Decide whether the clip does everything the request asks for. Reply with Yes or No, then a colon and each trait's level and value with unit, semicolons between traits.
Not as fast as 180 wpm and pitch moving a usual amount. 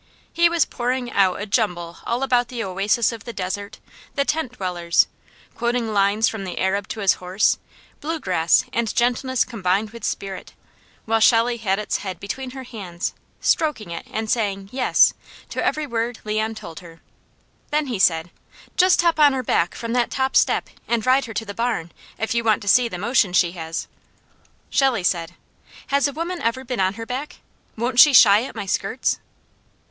No: average, 185 wpm; average, 4.6 semitones